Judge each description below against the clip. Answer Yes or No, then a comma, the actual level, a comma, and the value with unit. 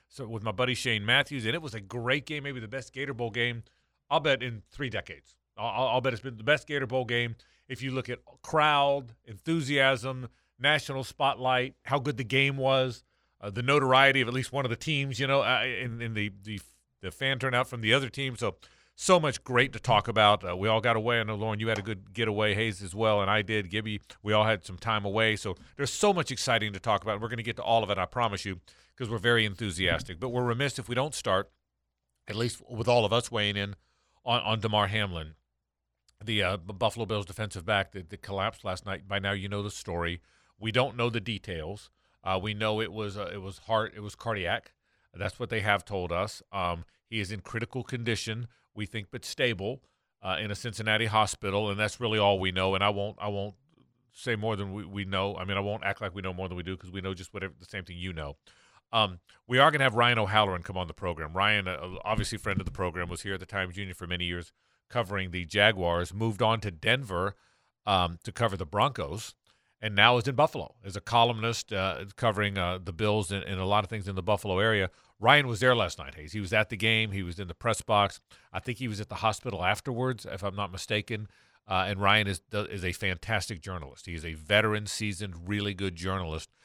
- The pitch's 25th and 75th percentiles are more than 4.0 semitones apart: No, average, 3.6 semitones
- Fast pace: Yes, fast, 240 wpm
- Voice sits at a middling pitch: No, low, 105 Hz